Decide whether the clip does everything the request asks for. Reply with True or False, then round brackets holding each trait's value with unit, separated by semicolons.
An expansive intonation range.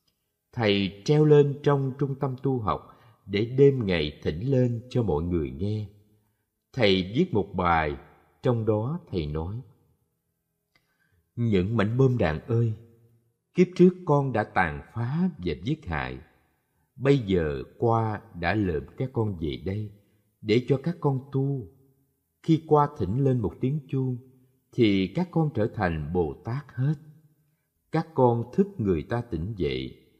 True (6.3 semitones)